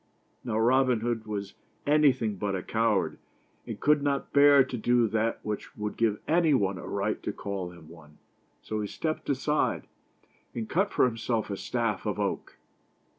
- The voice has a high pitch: No, low, 115 Hz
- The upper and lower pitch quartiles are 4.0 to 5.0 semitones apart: Yes, average, 4.6 semitones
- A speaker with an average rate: Yes, average, 170 wpm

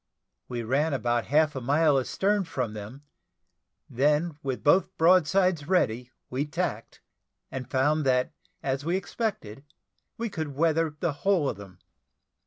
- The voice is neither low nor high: Yes, medium, 145 Hz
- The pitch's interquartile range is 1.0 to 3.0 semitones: No, average, 4.4 semitones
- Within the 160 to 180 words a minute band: No, average, 140 wpm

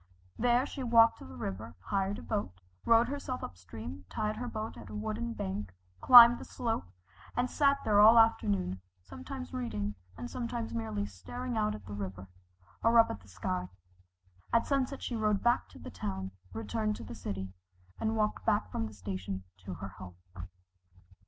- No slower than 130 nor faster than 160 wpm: No, average, 180 wpm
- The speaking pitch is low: Yes, low, 115 Hz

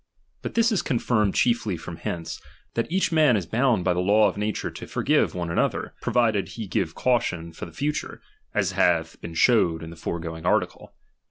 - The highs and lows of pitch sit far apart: Yes, wide, 6.2 semitones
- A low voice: Yes, low, 100 Hz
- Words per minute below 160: No, average, 200 wpm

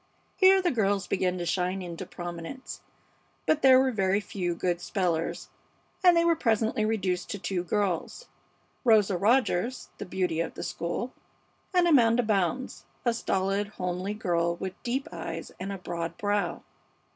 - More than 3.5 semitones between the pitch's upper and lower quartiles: Yes, average, 4.9 semitones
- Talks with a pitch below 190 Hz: No, high, 195 Hz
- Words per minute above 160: No, average, 155 wpm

